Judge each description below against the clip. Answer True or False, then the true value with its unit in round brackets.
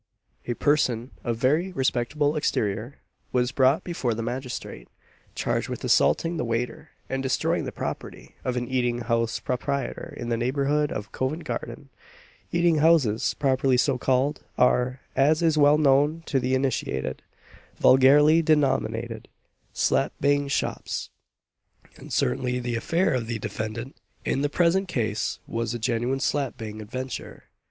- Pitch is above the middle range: False (130 Hz)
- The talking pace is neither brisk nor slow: True (145 wpm)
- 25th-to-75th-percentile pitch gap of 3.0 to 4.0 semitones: True (3.6 semitones)